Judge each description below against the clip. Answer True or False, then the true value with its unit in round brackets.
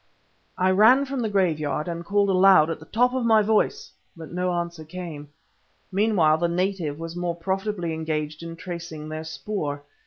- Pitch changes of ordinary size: True (4.0 semitones)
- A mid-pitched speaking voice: True (175 Hz)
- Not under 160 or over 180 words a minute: True (175 wpm)